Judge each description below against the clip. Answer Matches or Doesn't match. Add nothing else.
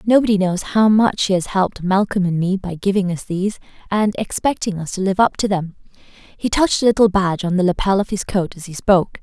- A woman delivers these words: Matches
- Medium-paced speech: Doesn't match